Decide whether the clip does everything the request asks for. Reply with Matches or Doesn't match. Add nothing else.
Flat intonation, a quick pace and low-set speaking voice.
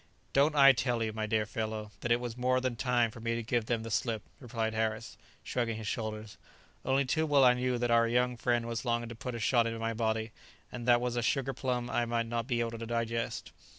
Matches